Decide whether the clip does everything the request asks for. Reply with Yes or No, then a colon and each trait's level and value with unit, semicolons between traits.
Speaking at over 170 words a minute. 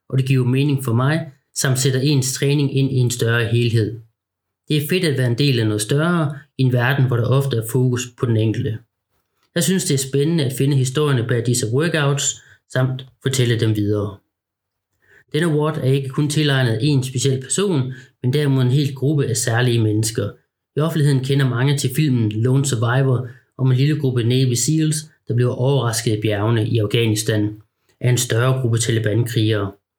Yes: average, 190 wpm